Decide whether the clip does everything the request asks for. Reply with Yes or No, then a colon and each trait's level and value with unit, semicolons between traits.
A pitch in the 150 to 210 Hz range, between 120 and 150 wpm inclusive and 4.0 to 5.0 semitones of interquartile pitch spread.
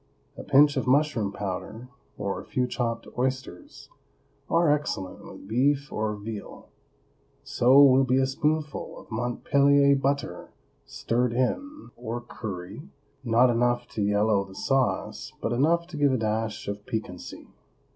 No: low, 125 Hz; average, 140 wpm; average, 4.3 semitones